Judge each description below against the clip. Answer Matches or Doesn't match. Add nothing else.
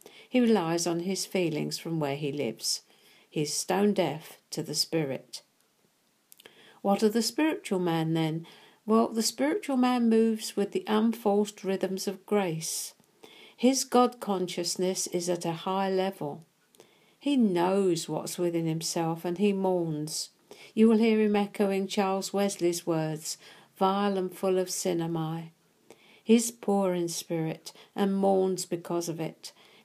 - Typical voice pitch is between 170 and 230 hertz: Matches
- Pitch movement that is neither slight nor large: Matches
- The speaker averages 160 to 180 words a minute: Doesn't match